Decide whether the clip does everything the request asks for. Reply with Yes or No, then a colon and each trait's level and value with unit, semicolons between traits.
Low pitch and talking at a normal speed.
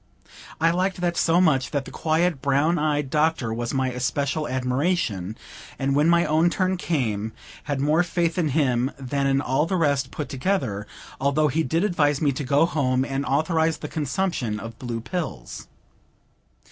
No: medium, 145 Hz; average, 170 wpm